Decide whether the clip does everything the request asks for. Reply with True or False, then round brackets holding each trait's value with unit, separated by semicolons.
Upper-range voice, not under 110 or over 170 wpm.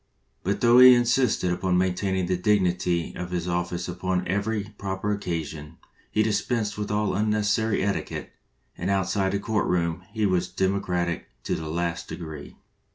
False (95 Hz; 155 wpm)